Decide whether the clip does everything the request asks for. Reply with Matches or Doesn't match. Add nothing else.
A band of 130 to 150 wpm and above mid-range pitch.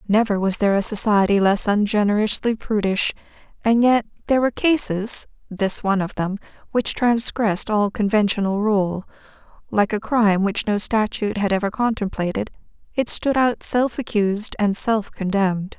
Matches